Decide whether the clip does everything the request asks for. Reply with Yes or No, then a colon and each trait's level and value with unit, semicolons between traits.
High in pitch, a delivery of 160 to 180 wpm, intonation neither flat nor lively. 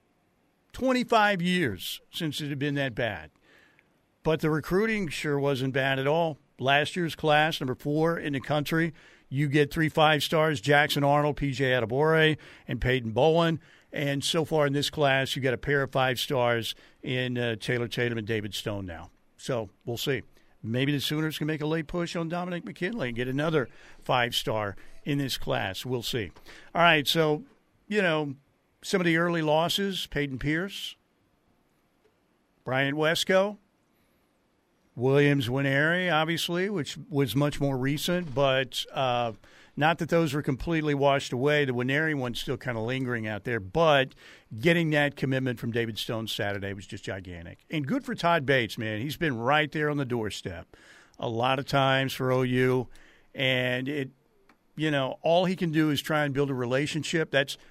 No: medium, 140 Hz; average, 175 wpm; average, 3.8 semitones